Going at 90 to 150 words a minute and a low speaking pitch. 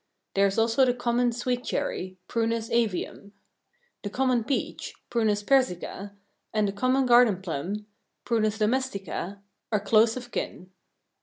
No: slow, 135 wpm; high, 225 Hz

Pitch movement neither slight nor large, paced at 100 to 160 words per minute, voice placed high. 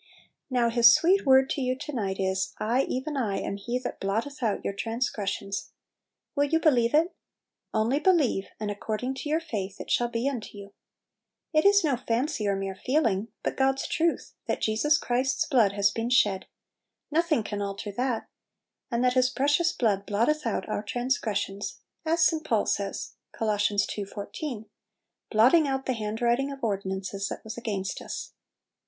No: average, 5.0 semitones; average, 175 wpm; high, 235 Hz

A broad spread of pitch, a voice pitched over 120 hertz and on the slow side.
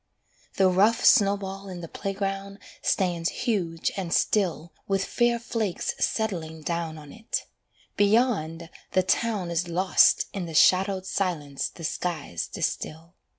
No: average, 3.2 semitones; medium, 185 Hz; slow, 130 wpm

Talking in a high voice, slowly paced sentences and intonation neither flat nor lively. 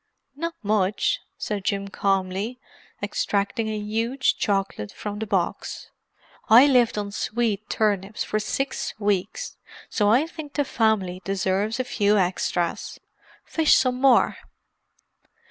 Yes: high, 210 Hz; slow, 125 wpm; average, 3.5 semitones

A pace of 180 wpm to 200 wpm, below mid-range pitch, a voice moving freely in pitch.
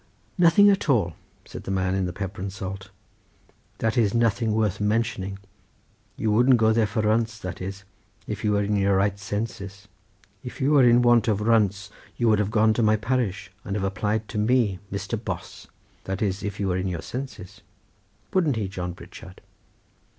No: average, 190 wpm; low, 105 Hz; average, 2.8 semitones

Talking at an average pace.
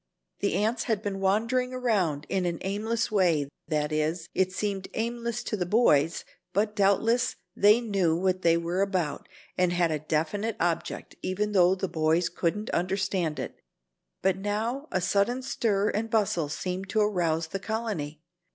Yes: average, 160 wpm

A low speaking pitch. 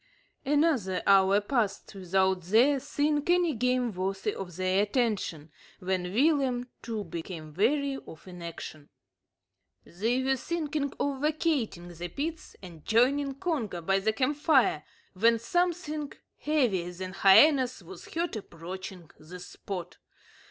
No: high, 220 Hz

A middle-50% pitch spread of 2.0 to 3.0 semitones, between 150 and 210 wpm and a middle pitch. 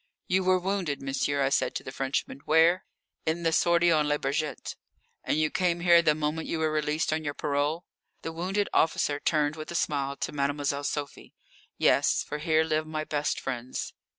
Yes: narrow, 2.5 semitones; average, 190 wpm; medium, 155 Hz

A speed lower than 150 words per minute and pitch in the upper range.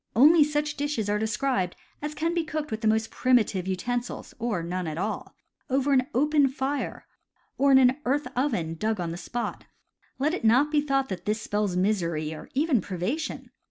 No: average, 190 wpm; high, 245 Hz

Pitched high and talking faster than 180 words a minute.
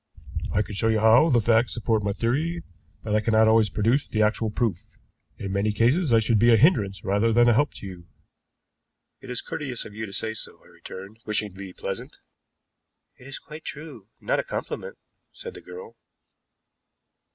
No: low, 110 Hz; average, 195 wpm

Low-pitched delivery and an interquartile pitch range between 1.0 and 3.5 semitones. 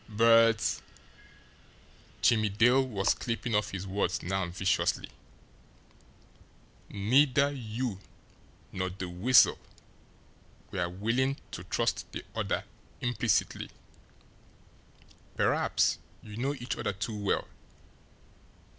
No: low, 110 Hz; average, 4.0 semitones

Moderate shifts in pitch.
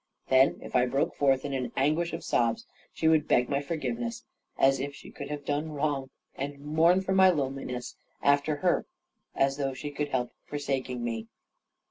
No: narrow, 2.3 semitones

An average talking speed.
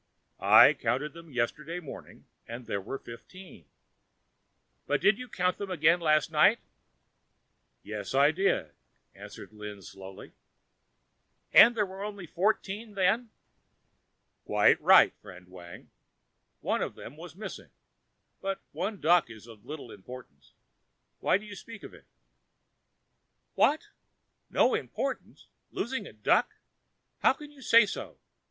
No: slow, 130 wpm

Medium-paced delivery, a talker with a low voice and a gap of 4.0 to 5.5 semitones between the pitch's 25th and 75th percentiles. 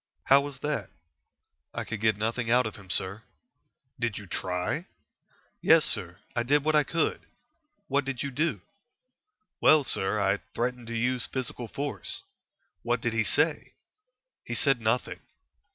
Yes: average, 150 wpm; low, 120 Hz; average, 4.6 semitones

